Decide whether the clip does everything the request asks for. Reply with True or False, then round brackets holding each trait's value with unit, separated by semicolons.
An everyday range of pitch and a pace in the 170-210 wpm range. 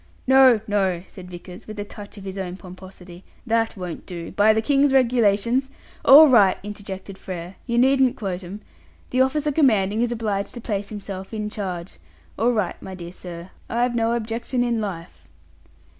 True (4.1 semitones; 175 wpm)